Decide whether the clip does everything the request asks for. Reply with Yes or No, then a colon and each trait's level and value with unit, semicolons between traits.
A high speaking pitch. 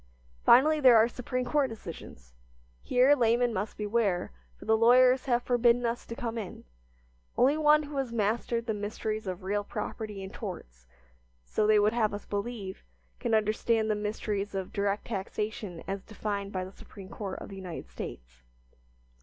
Yes: high, 215 Hz